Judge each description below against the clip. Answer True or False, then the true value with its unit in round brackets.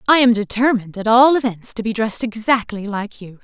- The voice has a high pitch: True (225 Hz)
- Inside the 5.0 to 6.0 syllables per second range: True (5.9 syllables/s)